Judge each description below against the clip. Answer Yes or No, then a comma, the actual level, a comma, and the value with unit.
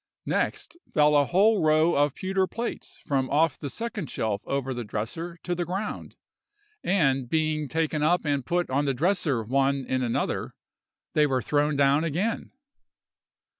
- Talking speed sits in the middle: Yes, average, 160 wpm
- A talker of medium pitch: Yes, medium, 150 Hz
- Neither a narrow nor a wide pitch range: Yes, average, 4.3 semitones